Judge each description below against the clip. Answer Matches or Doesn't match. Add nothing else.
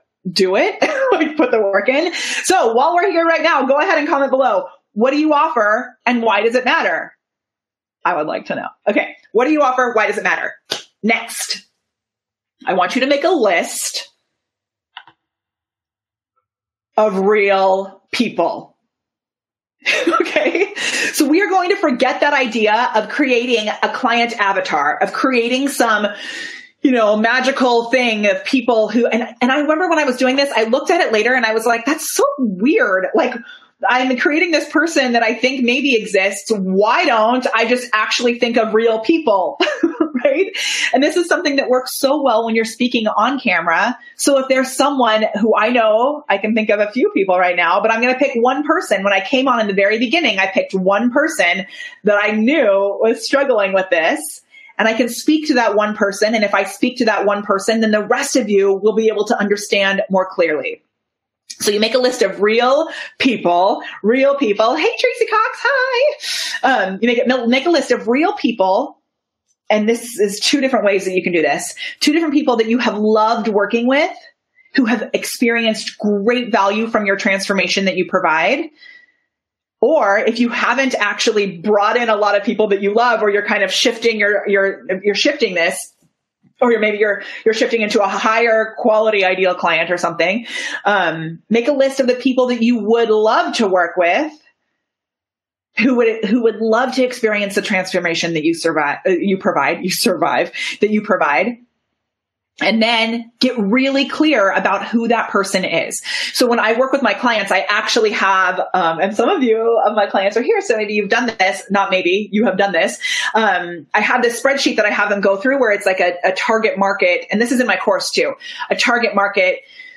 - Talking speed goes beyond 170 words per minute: Matches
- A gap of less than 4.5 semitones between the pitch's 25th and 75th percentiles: Doesn't match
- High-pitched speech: Matches